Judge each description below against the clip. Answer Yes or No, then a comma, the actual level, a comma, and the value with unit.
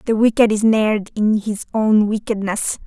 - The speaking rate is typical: Yes, average, 170 wpm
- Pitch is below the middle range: No, high, 215 Hz